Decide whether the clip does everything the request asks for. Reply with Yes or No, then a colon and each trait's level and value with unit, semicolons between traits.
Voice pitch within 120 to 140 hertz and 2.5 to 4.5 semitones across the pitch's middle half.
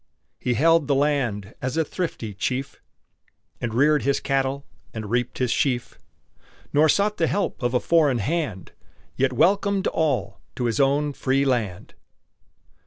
Yes: low, 135 Hz; average, 3.9 semitones